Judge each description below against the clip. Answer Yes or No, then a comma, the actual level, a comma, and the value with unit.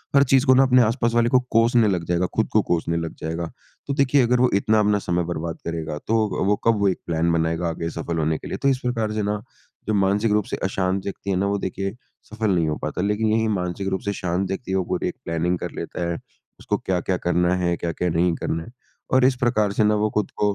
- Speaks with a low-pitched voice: Yes, very low, 95 Hz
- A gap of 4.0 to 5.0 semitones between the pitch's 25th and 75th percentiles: Yes, average, 4.3 semitones